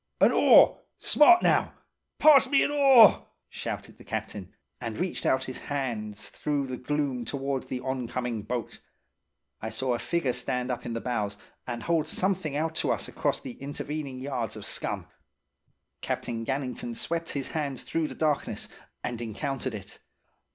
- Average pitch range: Yes, average, 4.1 semitones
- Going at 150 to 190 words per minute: Yes, average, 160 wpm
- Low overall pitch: Yes, low, 130 Hz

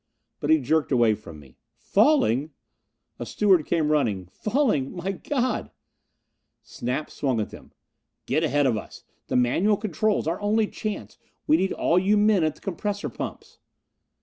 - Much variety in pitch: Yes, wide, 7.6 semitones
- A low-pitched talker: No, medium, 165 Hz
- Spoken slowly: No, average, 155 wpm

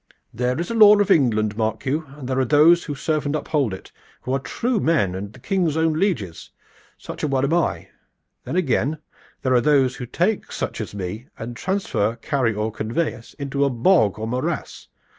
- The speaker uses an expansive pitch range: Yes, wide, 5.9 semitones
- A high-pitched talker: No, low, 135 Hz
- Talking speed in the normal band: No, fast, 210 wpm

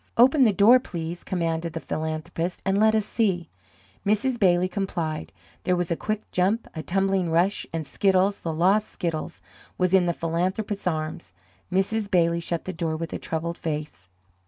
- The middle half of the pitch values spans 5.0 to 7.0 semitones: No, average, 3.4 semitones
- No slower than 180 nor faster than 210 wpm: No, average, 170 wpm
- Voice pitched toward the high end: No, medium, 180 Hz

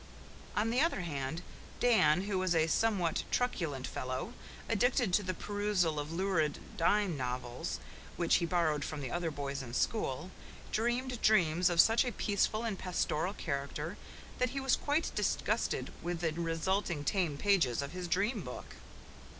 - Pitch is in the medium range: Yes, medium, 175 Hz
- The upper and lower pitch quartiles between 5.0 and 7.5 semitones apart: Yes, wide, 5.5 semitones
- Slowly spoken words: No, average, 160 wpm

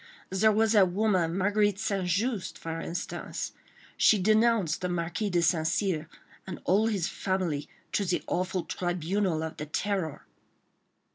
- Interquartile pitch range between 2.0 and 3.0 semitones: No, average, 3.5 semitones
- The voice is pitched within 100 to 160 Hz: No, medium, 185 Hz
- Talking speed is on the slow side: No, average, 145 wpm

